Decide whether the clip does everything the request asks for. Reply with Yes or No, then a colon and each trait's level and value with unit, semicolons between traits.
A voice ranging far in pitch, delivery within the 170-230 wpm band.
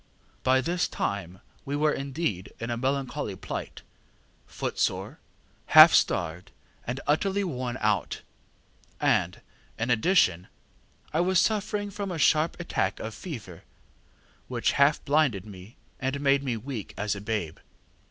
No: wide, 6.8 semitones; slow, 135 wpm